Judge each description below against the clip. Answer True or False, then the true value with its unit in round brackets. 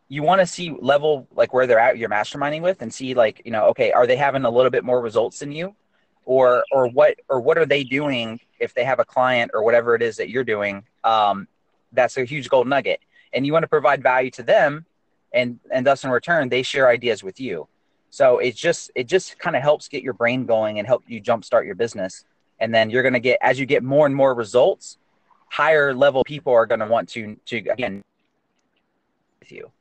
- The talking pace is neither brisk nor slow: False (230 wpm)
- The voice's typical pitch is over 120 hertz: True (135 Hz)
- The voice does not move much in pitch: False (4.1 semitones)